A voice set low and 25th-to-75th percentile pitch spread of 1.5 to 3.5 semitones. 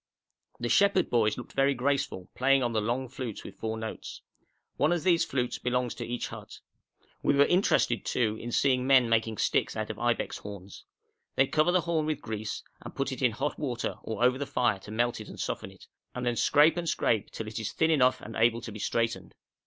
No: low, 120 Hz; average, 3.9 semitones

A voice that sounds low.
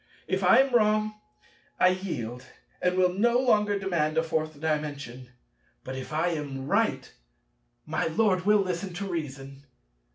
No: medium, 175 Hz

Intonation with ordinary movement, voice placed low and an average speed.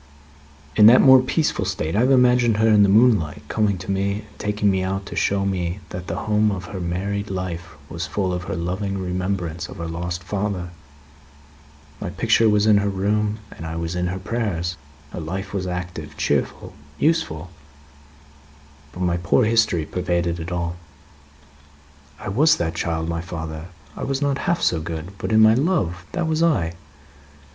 Yes: average, 3.5 semitones; very low, 95 Hz; average, 180 wpm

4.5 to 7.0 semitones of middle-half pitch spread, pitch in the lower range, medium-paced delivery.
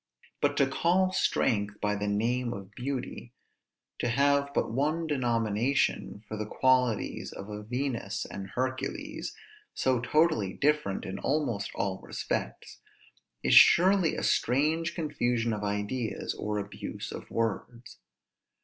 No: average, 5.2 semitones; low, 120 Hz; slow, 130 wpm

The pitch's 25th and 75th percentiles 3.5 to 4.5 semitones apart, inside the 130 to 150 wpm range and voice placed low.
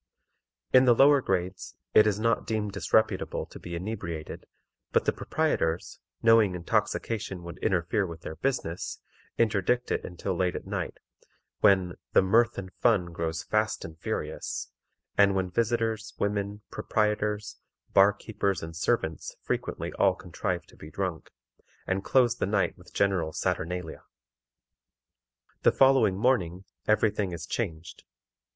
Yes: average, 3.8 semitones; average, 140 wpm; low, 100 Hz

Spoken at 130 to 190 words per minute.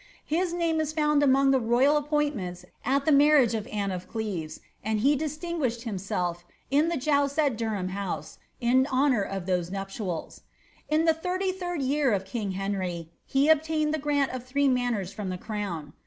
Yes: average, 165 wpm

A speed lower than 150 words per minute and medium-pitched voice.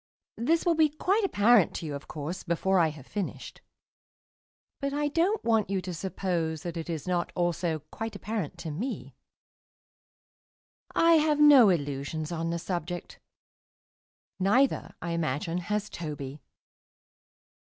Yes: average, 140 wpm; medium, 180 Hz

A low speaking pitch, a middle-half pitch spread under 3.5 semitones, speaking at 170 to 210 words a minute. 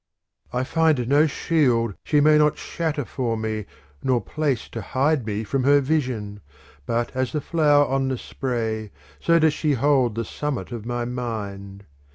No: low, 130 Hz; average, 4.3 semitones; average, 175 wpm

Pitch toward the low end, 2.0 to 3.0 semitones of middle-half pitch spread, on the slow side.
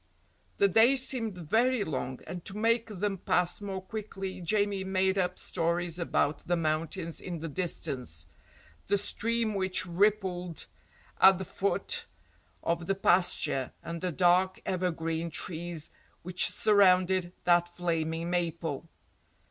No: medium, 180 Hz; narrow, 2.6 semitones; slow, 130 wpm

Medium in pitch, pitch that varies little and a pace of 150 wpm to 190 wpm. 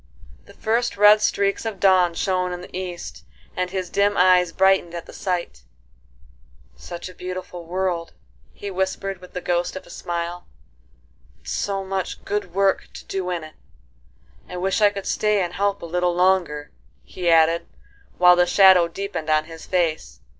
Yes: medium, 180 Hz; narrow, 2.0 semitones; average, 170 wpm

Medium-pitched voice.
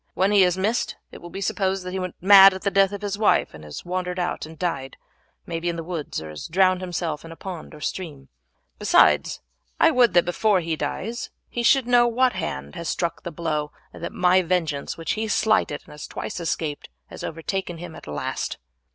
Yes: medium, 180 Hz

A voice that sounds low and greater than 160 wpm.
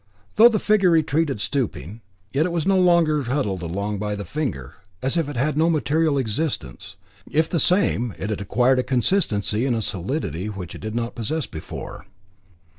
Yes: low, 130 Hz; average, 185 wpm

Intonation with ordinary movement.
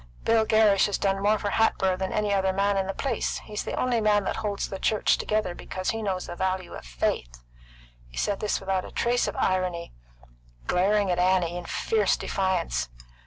No: narrow, 2.3 semitones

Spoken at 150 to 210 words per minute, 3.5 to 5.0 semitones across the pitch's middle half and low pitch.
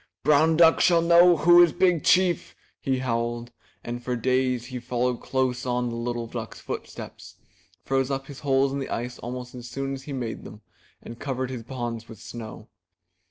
No: average, 185 wpm; narrow, 2.6 semitones; low, 130 Hz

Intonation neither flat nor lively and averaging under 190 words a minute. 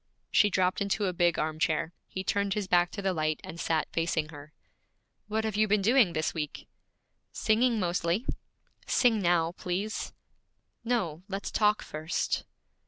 Yes: average, 4.3 semitones; average, 160 wpm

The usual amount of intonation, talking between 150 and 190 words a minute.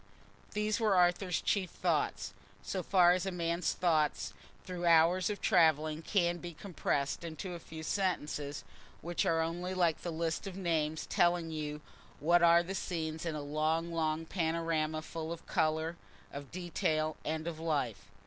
No: narrow, 2.1 semitones; average, 160 wpm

